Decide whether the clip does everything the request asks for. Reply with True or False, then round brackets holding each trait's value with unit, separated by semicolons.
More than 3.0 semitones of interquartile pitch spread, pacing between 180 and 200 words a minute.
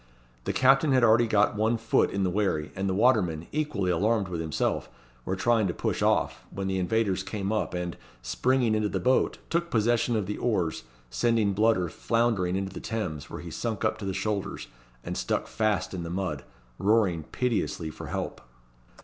True (3.8 semitones; 190 wpm)